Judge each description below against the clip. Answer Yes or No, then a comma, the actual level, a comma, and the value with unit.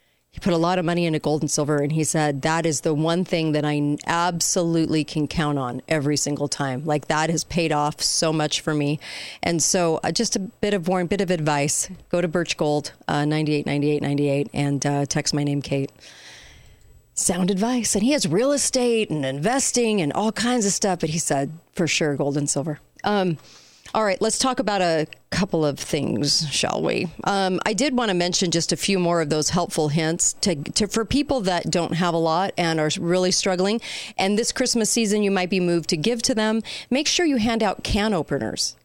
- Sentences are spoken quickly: Yes, fast, 220 wpm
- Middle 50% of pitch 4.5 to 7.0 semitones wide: Yes, average, 5.0 semitones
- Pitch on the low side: No, medium, 170 Hz